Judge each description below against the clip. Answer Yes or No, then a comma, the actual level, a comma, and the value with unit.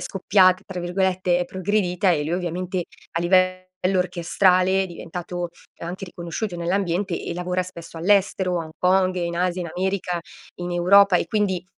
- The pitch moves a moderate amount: No, narrow, 1.4 semitones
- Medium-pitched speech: Yes, medium, 180 Hz